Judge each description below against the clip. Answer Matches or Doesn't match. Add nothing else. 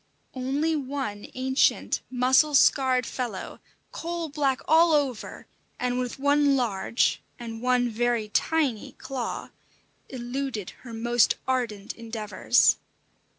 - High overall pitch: Matches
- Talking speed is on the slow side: Matches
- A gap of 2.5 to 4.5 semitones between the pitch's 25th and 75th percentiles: Matches